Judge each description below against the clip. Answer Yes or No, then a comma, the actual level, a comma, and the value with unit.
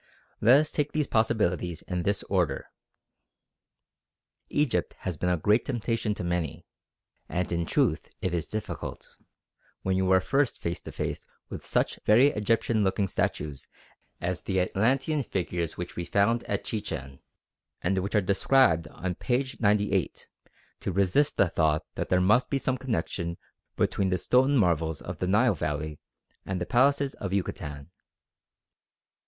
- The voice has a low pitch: Yes, very low, 95 Hz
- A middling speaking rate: Yes, average, 150 wpm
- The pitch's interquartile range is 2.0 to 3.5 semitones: No, average, 5.1 semitones